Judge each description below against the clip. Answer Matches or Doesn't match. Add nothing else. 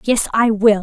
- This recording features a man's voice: Doesn't match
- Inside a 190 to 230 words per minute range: Matches